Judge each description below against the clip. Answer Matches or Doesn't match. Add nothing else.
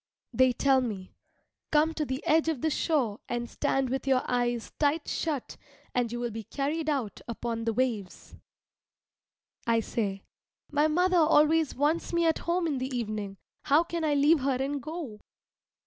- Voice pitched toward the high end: Matches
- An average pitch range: Matches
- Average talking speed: Matches